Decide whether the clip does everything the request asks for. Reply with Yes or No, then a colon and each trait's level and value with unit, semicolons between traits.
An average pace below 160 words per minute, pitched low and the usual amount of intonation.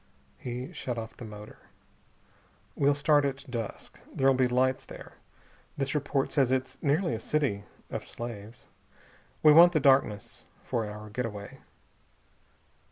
Yes: slow, 135 wpm; low, 130 Hz; average, 3.8 semitones